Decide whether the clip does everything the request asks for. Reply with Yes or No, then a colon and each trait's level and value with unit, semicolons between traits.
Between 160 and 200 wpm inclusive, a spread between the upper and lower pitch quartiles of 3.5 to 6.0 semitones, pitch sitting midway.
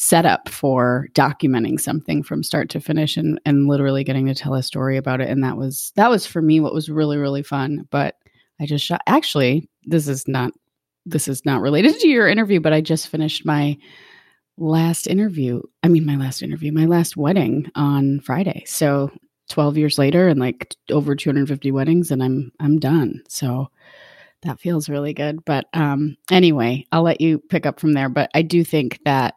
No: average, 195 wpm; average, 2.8 semitones; medium, 150 Hz